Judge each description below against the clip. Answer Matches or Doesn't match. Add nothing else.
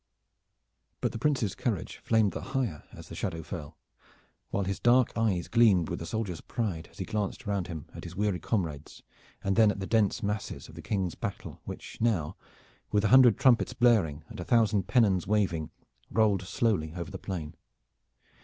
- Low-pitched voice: Matches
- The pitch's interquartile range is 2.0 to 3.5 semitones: Doesn't match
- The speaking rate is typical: Matches